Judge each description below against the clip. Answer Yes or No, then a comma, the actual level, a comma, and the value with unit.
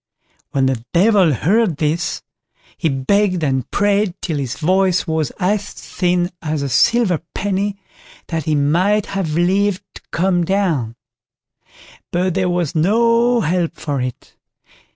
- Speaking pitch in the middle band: Yes, medium, 175 Hz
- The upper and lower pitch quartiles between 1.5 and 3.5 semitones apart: No, average, 4.4 semitones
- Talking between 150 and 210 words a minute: No, slow, 135 wpm